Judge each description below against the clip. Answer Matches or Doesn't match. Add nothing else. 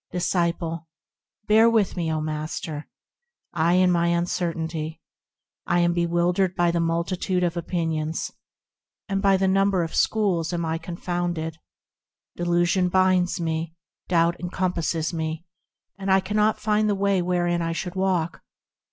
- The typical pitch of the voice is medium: Matches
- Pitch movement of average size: Doesn't match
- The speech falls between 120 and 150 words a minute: Matches